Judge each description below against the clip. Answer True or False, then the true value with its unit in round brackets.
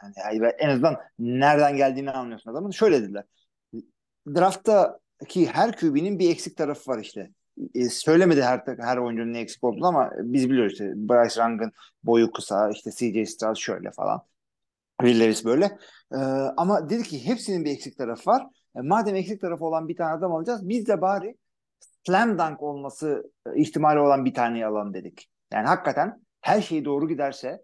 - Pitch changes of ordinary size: False (6.4 semitones)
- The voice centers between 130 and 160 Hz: True (140 Hz)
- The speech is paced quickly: True (165 wpm)